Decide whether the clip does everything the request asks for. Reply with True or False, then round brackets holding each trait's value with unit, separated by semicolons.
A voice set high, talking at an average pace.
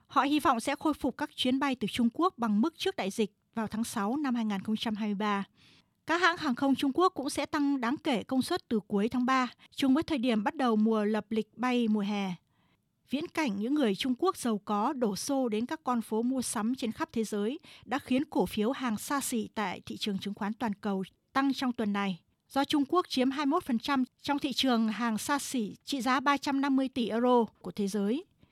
True (250 Hz; 225 wpm)